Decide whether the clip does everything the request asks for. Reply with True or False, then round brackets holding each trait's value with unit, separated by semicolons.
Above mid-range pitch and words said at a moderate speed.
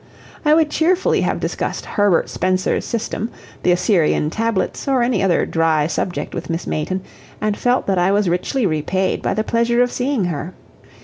True (195 Hz; 175 wpm)